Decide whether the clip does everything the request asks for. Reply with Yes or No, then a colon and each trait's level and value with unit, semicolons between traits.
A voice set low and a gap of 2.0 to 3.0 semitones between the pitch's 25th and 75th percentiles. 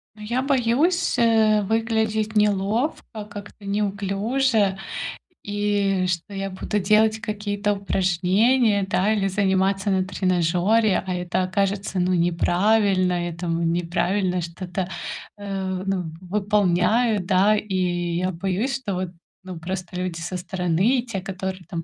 No: high, 195 Hz; narrow, 2.6 semitones